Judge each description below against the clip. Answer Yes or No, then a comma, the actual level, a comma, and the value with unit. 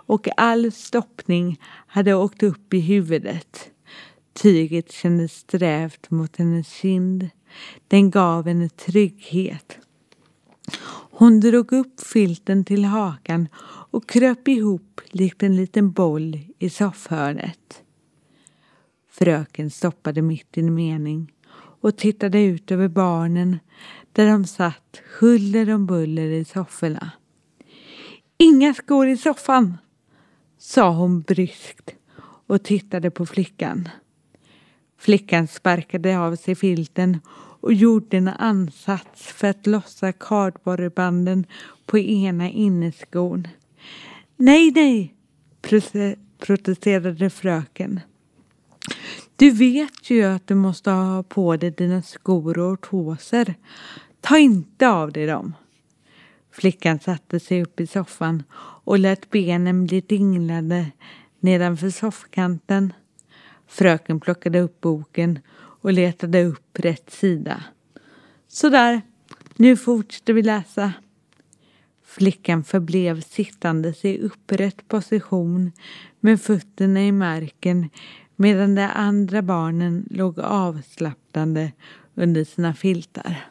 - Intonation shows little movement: No, average, 3.3 semitones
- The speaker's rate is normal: No, slow, 105 wpm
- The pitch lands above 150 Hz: Yes, medium, 185 Hz